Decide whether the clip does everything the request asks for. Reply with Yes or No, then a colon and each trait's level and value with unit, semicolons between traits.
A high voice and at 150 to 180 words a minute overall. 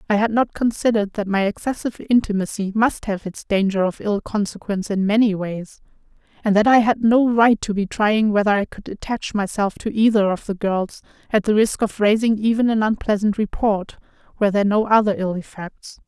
No: high, 210 Hz; average, 195 wpm